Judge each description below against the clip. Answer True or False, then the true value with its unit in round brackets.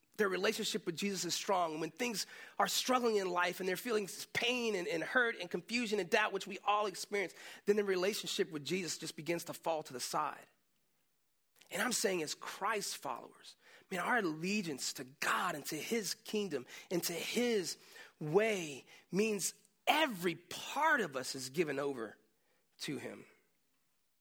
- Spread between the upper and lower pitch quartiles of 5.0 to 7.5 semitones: False (4.1 semitones)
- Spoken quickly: False (170 wpm)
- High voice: True (195 Hz)